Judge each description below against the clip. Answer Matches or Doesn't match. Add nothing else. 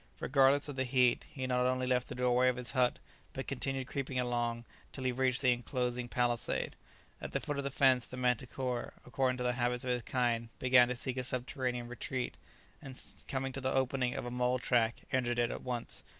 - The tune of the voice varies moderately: Doesn't match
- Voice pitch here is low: Matches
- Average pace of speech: Doesn't match